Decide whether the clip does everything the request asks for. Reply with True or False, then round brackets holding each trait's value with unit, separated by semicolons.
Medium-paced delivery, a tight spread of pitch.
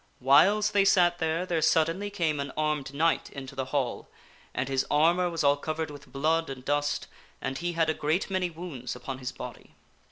False (195 wpm; 3.8 semitones)